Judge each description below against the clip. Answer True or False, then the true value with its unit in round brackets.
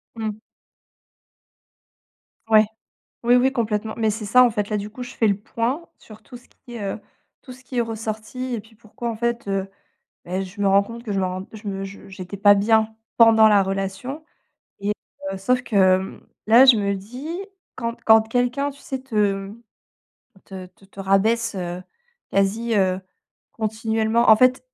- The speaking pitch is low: False (220 Hz)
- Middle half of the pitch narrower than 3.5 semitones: True (3.0 semitones)